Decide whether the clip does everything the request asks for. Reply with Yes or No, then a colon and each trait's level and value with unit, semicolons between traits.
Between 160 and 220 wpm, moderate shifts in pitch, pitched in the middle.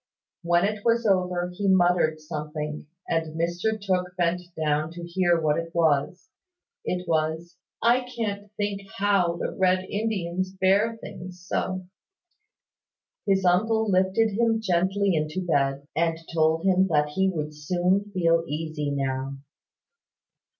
No: slow, 135 wpm; average, 3.3 semitones; medium, 180 Hz